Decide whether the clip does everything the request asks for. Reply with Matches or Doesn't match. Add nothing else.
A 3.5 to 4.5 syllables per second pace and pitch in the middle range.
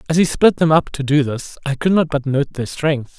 Doesn't match